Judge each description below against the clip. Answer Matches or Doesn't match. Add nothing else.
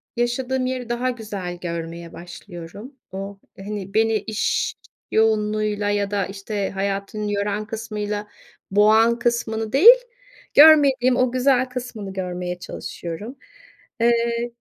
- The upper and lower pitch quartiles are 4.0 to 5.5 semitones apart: Doesn't match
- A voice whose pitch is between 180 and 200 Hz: Doesn't match